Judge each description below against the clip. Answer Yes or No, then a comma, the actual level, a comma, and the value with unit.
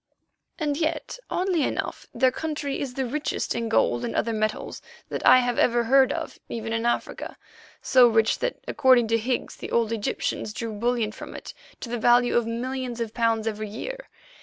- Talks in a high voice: Yes, high, 240 Hz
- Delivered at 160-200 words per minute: Yes, average, 185 wpm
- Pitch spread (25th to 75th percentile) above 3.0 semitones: No, average, 2.7 semitones